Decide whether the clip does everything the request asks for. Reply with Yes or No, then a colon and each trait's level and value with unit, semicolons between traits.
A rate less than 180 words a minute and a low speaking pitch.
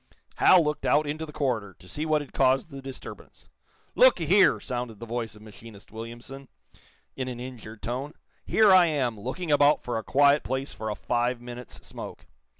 No: average, 190 wpm; low, 130 Hz